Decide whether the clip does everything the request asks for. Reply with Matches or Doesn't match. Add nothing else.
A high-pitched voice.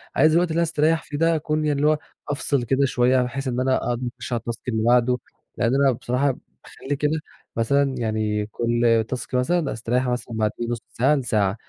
Doesn't match